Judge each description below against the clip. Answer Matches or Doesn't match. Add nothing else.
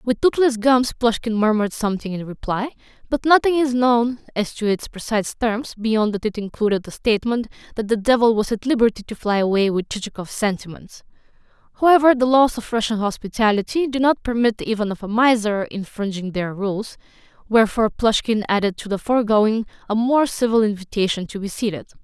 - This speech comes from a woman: Matches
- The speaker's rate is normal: Matches